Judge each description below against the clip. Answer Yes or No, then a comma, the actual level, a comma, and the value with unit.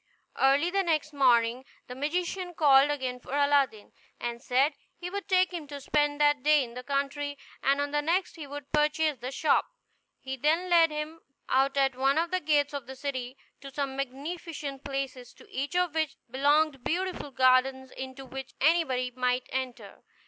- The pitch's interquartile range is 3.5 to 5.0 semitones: No, average, 2.7 semitones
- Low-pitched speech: No, very high, 280 Hz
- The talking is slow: No, average, 180 wpm